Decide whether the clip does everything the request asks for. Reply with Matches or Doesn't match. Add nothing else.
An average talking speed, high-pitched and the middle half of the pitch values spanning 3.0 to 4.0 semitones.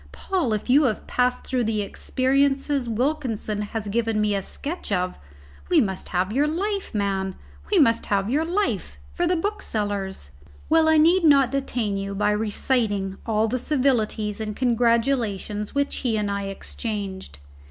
Doesn't match